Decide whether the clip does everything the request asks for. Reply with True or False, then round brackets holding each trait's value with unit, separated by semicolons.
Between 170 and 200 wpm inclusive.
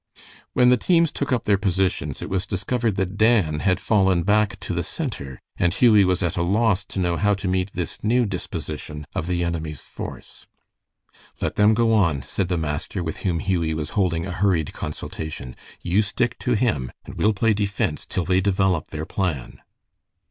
True (190 wpm)